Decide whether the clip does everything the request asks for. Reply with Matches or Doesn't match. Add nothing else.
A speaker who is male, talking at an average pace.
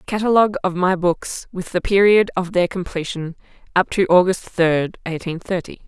Doesn't match